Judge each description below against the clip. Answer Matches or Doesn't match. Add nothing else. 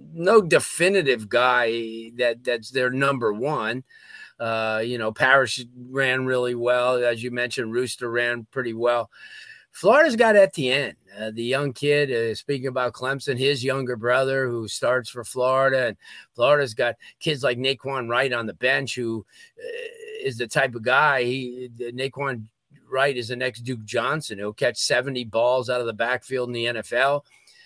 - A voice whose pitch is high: Doesn't match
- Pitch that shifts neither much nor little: Doesn't match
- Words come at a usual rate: Matches